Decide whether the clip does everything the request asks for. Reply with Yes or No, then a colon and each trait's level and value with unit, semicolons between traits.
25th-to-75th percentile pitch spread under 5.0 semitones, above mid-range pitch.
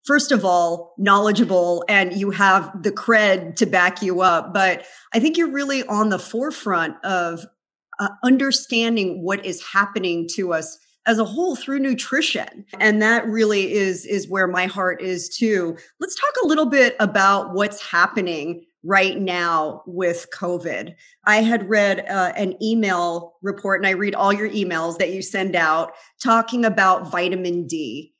Yes: average, 3.5 semitones; high, 195 Hz